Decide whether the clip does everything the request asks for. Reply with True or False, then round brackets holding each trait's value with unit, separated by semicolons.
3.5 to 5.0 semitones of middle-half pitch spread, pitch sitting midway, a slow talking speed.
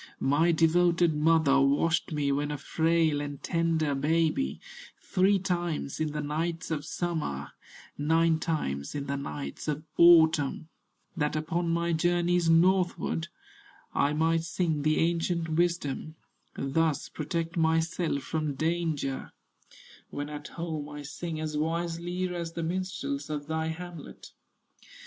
False (2.4 semitones; 160 Hz; 130 wpm)